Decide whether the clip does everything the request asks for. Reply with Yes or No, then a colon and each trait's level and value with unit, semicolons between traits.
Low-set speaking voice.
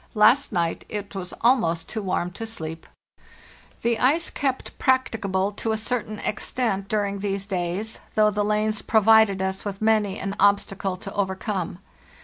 No: high, 205 Hz